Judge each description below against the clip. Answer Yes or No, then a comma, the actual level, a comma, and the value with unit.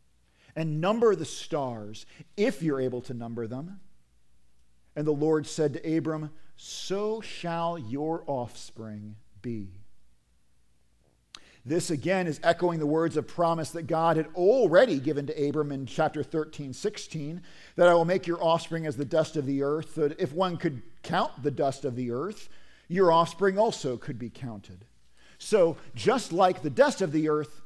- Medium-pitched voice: Yes, medium, 155 Hz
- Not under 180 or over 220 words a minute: No, average, 165 wpm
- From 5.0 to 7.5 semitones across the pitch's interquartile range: Yes, average, 5.3 semitones